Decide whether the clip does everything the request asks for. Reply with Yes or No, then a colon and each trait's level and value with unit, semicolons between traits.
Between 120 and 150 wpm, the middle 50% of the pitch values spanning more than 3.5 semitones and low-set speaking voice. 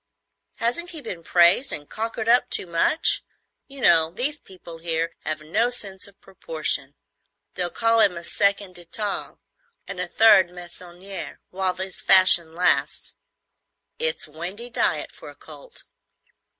No: average, 145 wpm; average, 4.8 semitones; high, 190 Hz